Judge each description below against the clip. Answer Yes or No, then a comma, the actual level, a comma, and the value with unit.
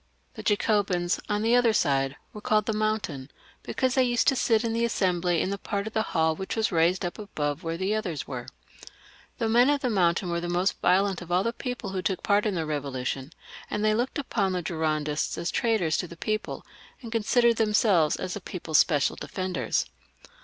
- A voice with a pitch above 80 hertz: Yes, high, 190 Hz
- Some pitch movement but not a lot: Yes, average, 4.7 semitones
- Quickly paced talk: Yes, fast, 215 wpm